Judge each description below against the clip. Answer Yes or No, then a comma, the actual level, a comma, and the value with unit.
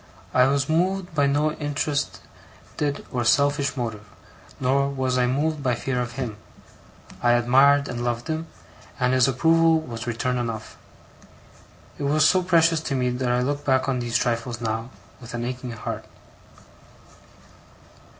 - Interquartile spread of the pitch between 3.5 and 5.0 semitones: No, average, 3.1 semitones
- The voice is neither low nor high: No, low, 130 Hz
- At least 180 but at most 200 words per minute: No, average, 150 wpm